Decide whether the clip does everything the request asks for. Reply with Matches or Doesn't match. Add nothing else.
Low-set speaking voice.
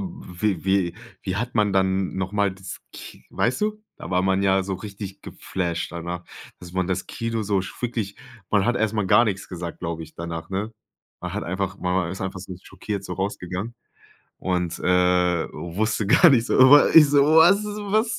Matches